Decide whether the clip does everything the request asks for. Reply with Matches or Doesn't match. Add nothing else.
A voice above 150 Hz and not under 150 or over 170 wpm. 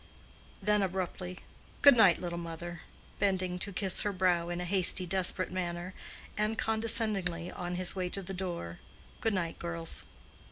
Matches